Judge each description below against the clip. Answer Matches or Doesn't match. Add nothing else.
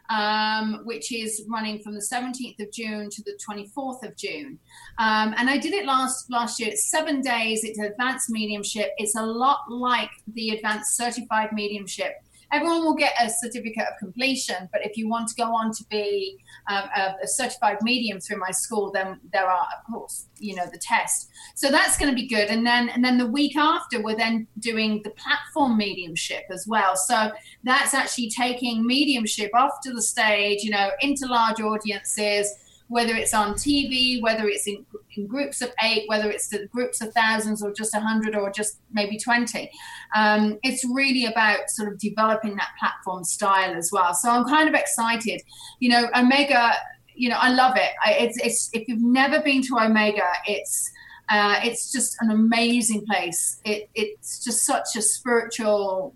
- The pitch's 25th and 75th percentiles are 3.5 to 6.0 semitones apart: Doesn't match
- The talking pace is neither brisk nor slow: Matches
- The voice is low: Doesn't match